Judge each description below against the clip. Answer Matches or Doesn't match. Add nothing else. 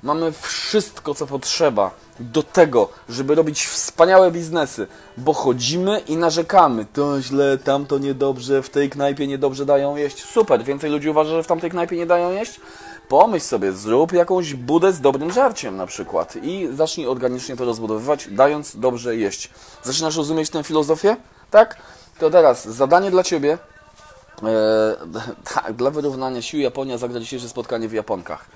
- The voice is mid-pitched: Matches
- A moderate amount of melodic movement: Matches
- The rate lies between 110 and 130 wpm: Doesn't match